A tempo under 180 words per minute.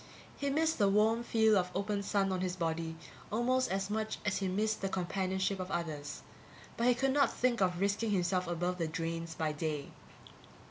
No: average, 190 wpm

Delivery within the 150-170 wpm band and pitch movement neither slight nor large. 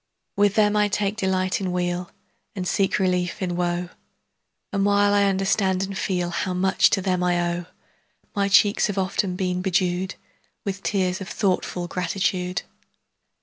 No: average, 160 wpm; narrow, 1.7 semitones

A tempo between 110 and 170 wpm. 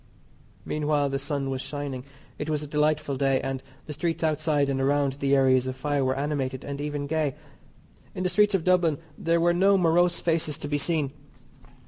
No: average, 190 wpm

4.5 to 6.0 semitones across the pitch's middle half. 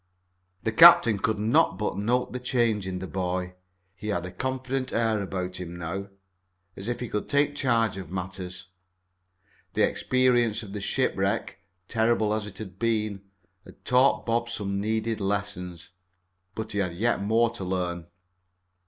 No: average, 3.8 semitones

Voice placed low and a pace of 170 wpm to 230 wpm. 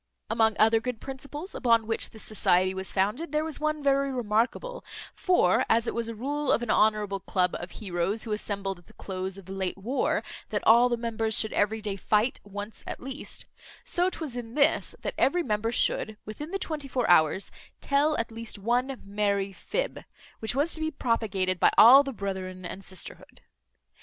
No: high, 225 Hz; average, 190 wpm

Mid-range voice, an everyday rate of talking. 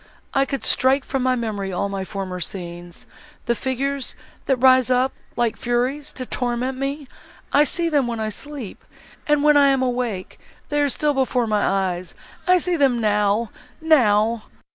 No: very high, 250 Hz; average, 155 wpm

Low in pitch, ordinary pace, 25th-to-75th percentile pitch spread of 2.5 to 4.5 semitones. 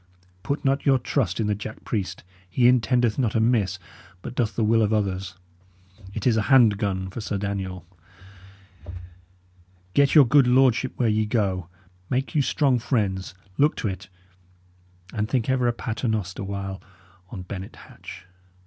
Yes: low, 110 Hz; average, 160 wpm; average, 4.2 semitones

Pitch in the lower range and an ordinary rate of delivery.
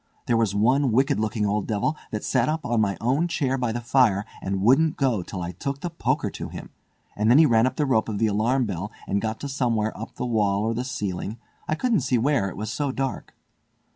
No: low, 115 Hz; fast, 235 wpm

